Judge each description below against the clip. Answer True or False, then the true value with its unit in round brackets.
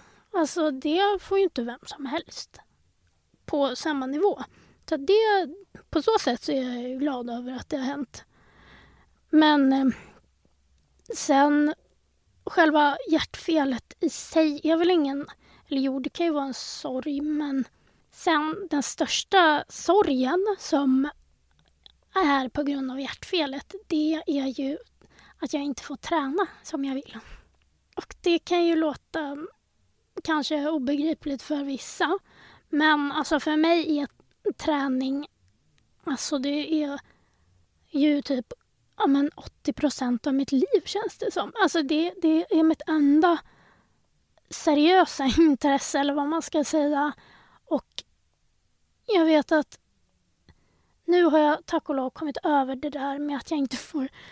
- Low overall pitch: False (300 Hz)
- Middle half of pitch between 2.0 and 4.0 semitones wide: True (2.9 semitones)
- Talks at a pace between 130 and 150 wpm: True (140 wpm)